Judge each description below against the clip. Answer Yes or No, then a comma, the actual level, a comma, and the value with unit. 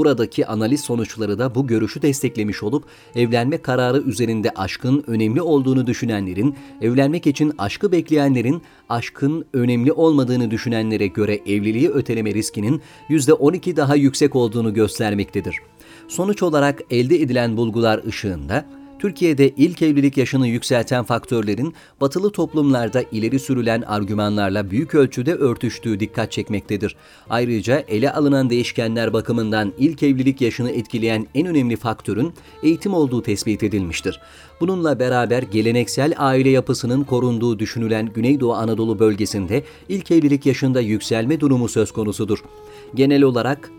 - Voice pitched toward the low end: Yes, low, 125 Hz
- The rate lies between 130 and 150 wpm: No, average, 120 wpm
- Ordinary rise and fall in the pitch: Yes, average, 4.3 semitones